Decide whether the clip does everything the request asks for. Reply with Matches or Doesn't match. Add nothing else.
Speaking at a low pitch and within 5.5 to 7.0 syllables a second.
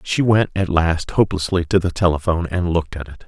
Matches